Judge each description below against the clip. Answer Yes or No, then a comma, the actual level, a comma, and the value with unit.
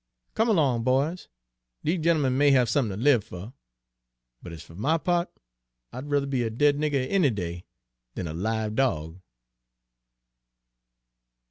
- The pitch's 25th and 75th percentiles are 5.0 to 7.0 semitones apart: Yes, wide, 5.5 semitones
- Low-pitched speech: Yes, low, 130 Hz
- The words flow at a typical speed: Yes, average, 145 wpm